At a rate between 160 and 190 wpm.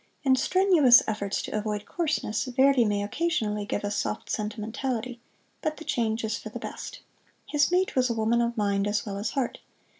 Yes: average, 185 wpm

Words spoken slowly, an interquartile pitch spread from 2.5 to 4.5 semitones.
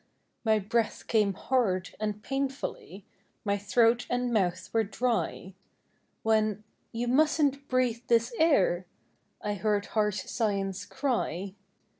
Yes: slow, 125 wpm; average, 3.5 semitones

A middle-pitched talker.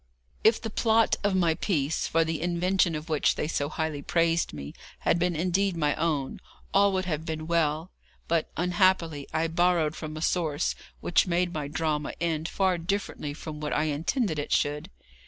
Yes: medium, 165 Hz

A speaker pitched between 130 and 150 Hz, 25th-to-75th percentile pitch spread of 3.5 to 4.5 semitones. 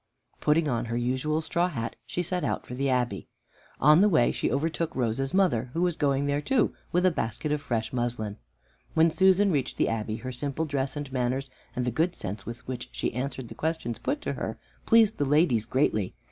No: medium, 140 Hz; average, 5.0 semitones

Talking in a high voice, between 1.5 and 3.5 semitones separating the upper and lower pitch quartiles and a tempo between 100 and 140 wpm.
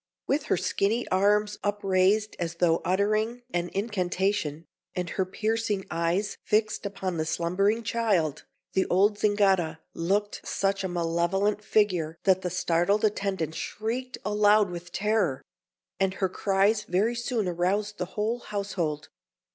Yes: high, 195 Hz; average, 3.0 semitones; slow, 135 wpm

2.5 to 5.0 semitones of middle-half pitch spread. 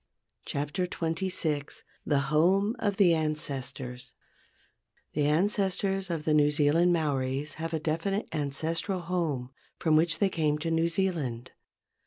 Yes: average, 3.5 semitones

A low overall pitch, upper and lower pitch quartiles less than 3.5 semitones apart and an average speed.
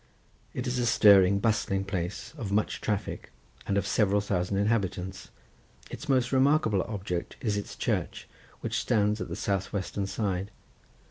Yes: low, 100 Hz; narrow, 2.6 semitones; average, 150 wpm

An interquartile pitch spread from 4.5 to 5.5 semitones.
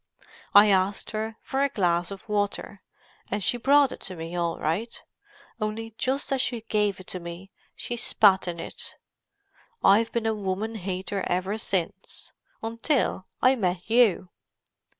No: average, 3.5 semitones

